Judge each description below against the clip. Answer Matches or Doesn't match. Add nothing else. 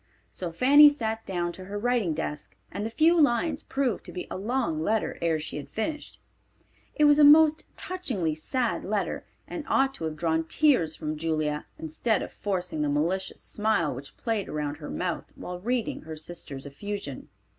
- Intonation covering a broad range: Matches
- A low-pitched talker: Doesn't match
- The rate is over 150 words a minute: Matches